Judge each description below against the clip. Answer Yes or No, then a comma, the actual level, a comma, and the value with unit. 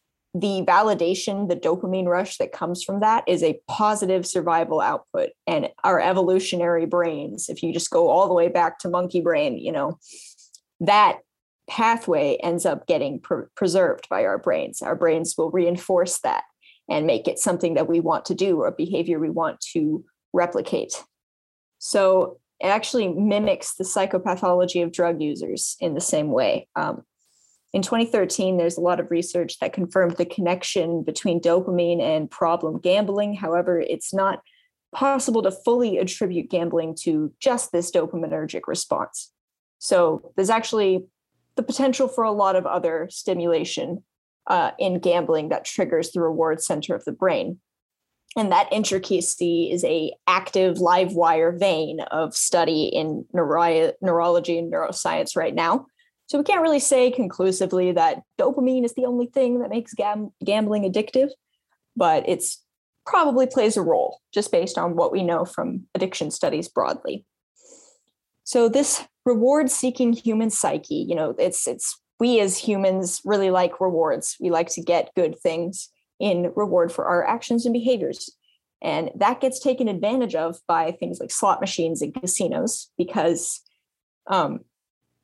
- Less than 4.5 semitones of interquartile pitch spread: No, average, 5.2 semitones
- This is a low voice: No, medium, 185 Hz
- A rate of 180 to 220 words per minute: No, average, 155 wpm